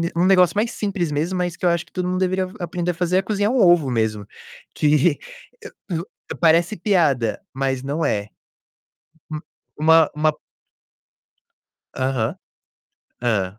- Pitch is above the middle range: No, medium, 165 Hz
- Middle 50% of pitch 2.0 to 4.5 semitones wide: No, average, 5.1 semitones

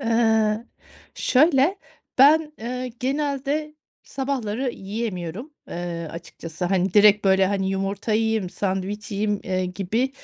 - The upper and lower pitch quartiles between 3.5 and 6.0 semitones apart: Yes, average, 5.1 semitones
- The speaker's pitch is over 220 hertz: No, high, 215 Hz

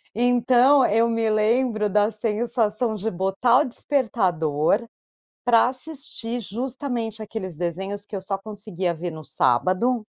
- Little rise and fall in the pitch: No, average, 4.0 semitones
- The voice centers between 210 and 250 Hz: Yes, high, 220 Hz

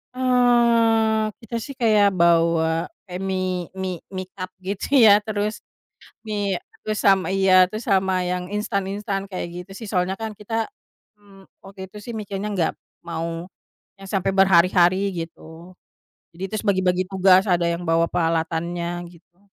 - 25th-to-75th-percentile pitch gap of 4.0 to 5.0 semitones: No, average, 2.8 semitones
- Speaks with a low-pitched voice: No, high, 190 Hz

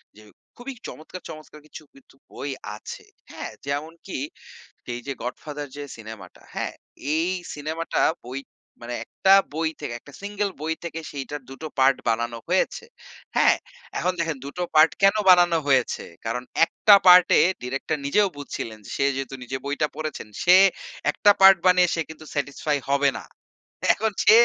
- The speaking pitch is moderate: Yes, medium, 150 Hz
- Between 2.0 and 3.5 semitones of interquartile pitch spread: No, average, 4.7 semitones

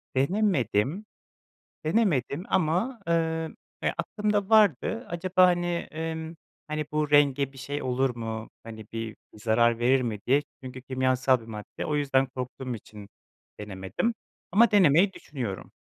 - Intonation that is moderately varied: No, wide, 6.3 semitones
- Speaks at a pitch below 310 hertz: Yes, low, 135 Hz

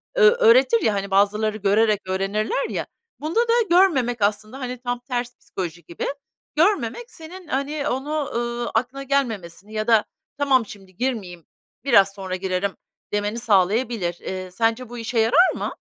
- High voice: Yes, high, 230 Hz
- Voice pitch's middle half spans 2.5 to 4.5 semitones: No, wide, 5.5 semitones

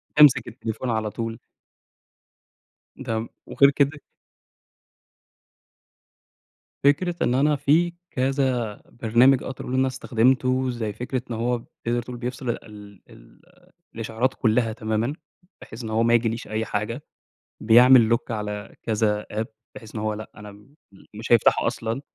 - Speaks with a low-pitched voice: Yes, low, 115 Hz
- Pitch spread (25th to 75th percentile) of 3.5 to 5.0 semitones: No, average, 2.9 semitones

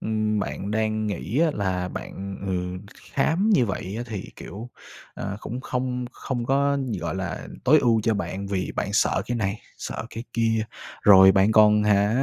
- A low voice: Yes, low, 110 Hz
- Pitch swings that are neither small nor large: Yes, average, 3.7 semitones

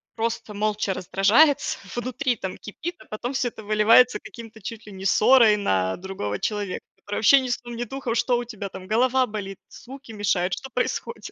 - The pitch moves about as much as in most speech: Yes, average, 3.6 semitones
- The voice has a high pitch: Yes, high, 220 Hz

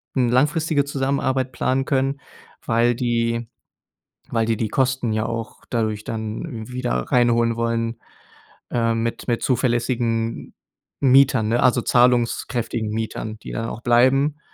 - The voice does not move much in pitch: Yes, narrow, 2.2 semitones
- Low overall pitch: Yes, low, 120 Hz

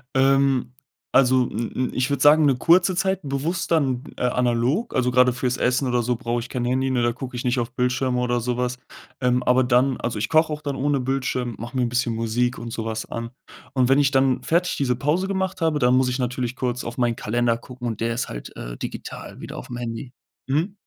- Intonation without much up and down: Yes, narrow, 2.0 semitones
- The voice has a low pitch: Yes, low, 125 Hz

